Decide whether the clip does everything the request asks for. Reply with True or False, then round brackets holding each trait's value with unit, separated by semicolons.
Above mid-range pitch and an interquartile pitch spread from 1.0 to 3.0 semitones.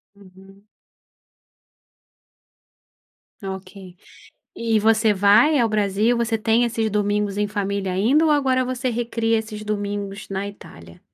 True (210 Hz; 2.5 semitones)